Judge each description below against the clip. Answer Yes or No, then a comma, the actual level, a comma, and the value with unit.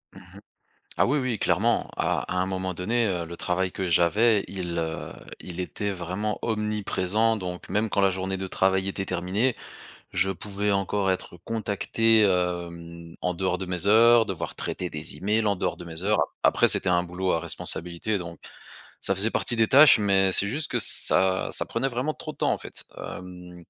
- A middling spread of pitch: Yes, average, 3.0 semitones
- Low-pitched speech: Yes, very low, 95 Hz